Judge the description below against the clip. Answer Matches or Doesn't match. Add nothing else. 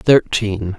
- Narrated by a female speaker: Doesn't match